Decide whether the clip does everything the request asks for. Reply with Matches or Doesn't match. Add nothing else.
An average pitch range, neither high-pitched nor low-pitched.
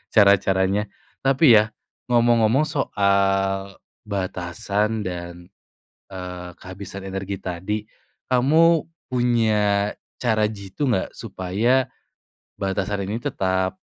Doesn't match